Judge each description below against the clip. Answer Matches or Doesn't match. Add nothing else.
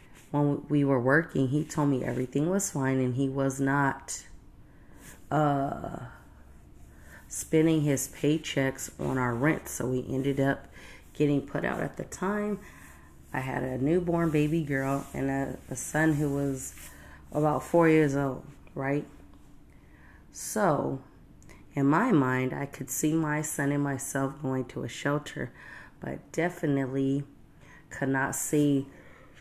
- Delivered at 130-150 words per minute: Matches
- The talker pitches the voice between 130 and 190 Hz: Matches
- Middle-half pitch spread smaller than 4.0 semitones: Matches